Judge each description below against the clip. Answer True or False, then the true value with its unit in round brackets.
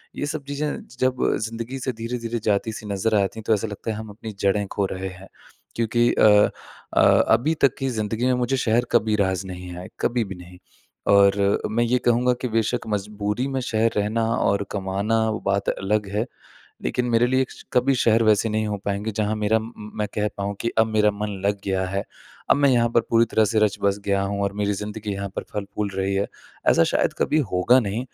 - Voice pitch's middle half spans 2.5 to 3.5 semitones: True (2.8 semitones)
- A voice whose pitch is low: True (110 Hz)